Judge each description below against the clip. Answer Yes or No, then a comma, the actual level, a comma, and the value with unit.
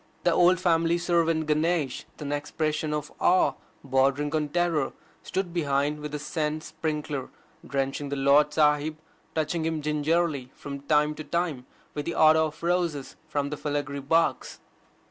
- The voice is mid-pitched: Yes, medium, 150 Hz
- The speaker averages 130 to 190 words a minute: Yes, average, 155 wpm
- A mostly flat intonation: Yes, narrow, 2.2 semitones